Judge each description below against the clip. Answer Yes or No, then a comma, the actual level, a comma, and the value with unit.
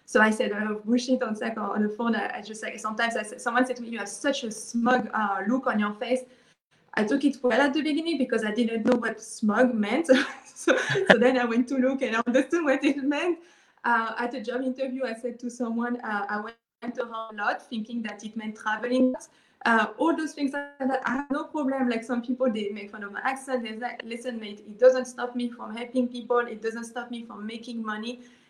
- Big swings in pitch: No, narrow, 2.5 semitones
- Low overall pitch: No, high, 245 Hz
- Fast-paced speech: Yes, fast, 255 wpm